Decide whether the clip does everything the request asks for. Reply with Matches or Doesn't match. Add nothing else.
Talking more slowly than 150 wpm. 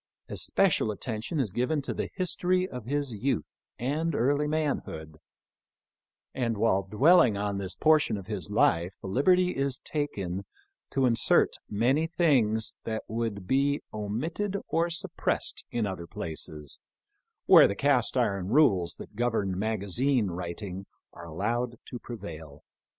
Matches